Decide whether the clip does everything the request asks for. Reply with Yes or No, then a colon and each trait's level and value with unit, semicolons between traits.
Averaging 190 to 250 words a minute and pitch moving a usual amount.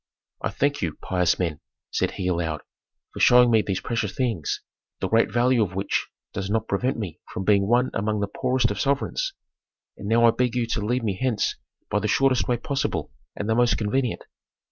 Yes: average, 200 wpm; average, 4.0 semitones